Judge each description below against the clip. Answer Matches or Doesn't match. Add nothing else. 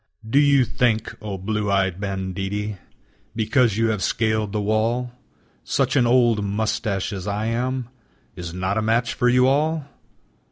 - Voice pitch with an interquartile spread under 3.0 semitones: Doesn't match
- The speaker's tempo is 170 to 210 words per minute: Doesn't match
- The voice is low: Matches